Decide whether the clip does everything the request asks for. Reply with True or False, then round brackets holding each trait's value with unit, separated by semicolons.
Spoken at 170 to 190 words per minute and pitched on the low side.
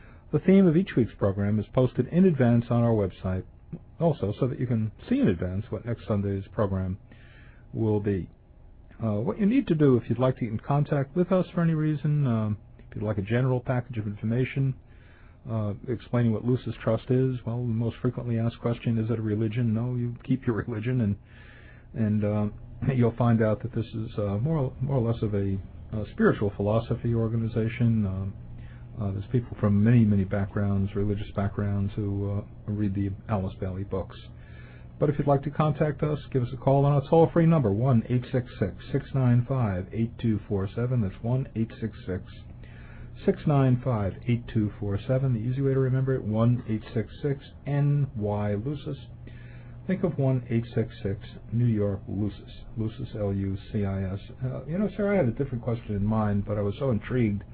True (180 wpm; 115 Hz)